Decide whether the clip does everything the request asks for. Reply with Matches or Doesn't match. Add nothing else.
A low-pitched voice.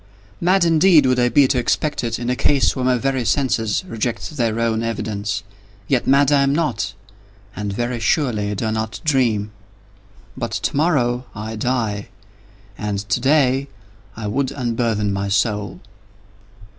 Matches